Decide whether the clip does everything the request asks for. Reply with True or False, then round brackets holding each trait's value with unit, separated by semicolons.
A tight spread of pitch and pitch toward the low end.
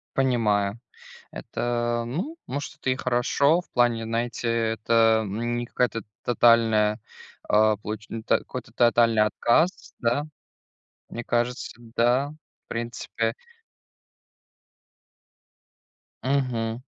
True (1.6 semitones; 120 Hz)